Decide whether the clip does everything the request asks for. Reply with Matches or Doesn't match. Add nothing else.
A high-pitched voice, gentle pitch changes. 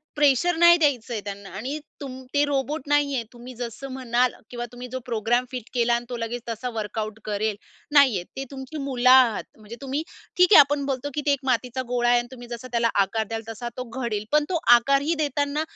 Doesn't match